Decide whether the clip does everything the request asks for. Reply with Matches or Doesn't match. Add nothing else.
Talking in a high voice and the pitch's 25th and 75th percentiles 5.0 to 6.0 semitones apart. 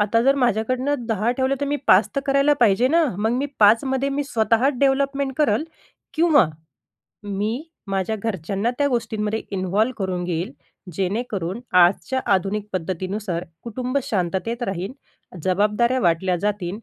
Matches